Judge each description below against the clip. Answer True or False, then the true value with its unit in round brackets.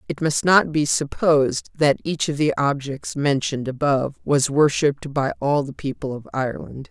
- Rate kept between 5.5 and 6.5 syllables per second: False (5.0 syllables/s)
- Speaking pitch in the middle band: True (145 Hz)